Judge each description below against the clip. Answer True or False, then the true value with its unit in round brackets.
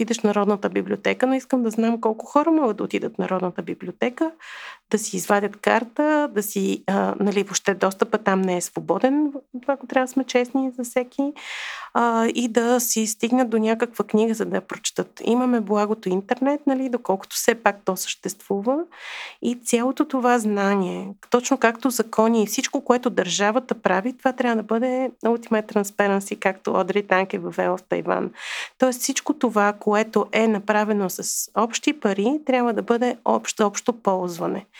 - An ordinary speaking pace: False (170 wpm)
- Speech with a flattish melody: False (3.9 semitones)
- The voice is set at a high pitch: True (225 Hz)